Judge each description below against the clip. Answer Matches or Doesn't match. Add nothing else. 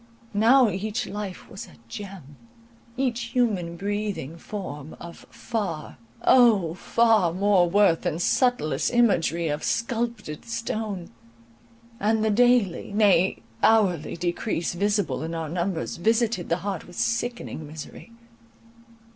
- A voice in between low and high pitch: Doesn't match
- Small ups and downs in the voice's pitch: Doesn't match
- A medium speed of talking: Doesn't match